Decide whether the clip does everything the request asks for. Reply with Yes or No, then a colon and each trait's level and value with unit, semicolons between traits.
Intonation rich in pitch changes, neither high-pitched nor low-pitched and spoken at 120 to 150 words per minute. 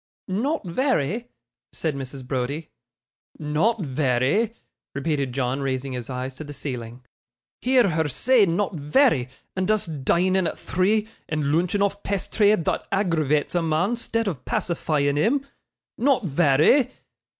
Yes: wide, 6.7 semitones; medium, 160 Hz; slow, 135 wpm